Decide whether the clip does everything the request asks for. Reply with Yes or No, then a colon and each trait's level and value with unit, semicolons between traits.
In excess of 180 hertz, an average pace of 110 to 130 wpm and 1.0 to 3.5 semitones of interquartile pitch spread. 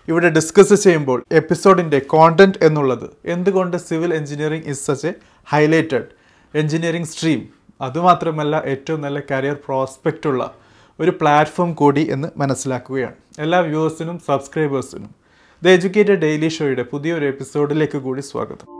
No: medium, 155 Hz; average, 120 wpm; average, 3.0 semitones